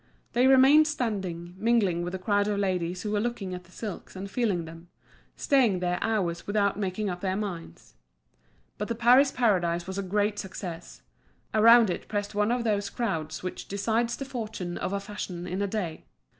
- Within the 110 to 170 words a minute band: No, average, 185 wpm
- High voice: Yes, high, 200 Hz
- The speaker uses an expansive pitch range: No, average, 3.8 semitones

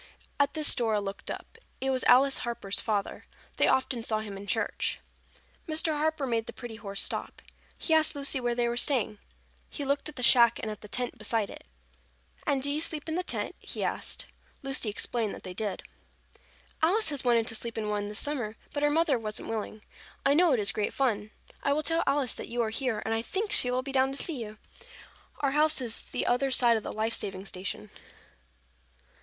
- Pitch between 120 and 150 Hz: No, high, 245 Hz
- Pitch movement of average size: Yes, average, 4.8 semitones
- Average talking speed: No, fast, 215 wpm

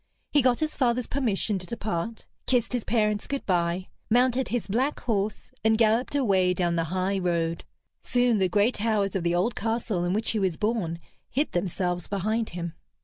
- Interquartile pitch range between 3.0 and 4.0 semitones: No, average, 4.6 semitones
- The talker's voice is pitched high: Yes, high, 210 Hz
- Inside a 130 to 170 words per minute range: No, average, 185 wpm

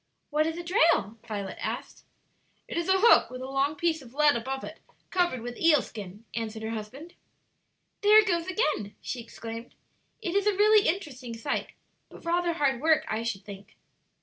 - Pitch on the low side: No, very high, 275 Hz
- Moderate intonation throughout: No, wide, 7.1 semitones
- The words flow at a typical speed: Yes, average, 185 wpm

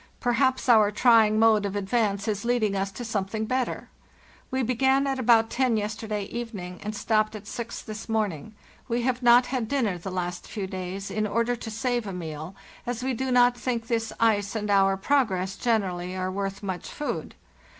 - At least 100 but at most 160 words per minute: No, average, 185 wpm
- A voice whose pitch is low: No, high, 220 Hz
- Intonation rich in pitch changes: No, average, 3.6 semitones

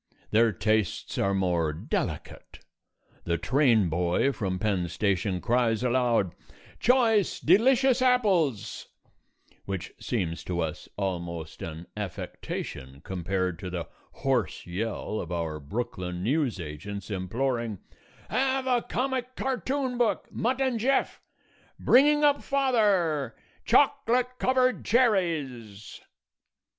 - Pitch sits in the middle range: No, low, 115 Hz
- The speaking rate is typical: No, slow, 110 wpm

